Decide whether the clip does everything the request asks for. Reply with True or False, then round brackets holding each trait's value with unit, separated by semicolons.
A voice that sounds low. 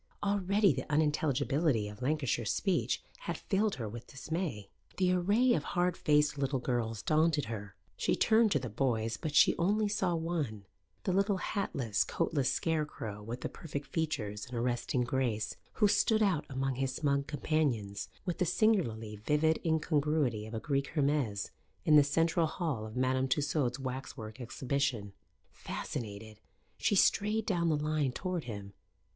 False (145 Hz)